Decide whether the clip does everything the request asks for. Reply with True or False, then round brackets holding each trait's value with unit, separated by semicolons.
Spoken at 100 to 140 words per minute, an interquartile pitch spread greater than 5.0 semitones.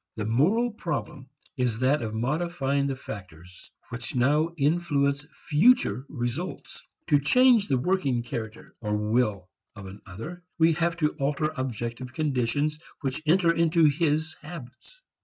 True (135 wpm; 5.4 semitones)